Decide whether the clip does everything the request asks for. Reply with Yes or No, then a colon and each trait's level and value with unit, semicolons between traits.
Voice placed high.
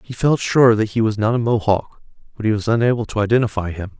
No: low, 110 Hz